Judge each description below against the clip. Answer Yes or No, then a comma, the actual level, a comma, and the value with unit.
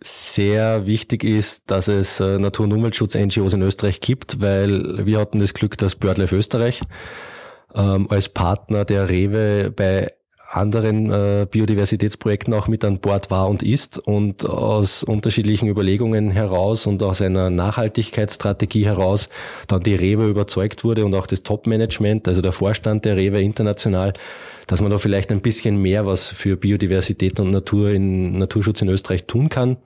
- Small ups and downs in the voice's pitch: Yes, narrow, 1.8 semitones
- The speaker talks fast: No, average, 155 wpm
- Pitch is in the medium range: No, low, 105 Hz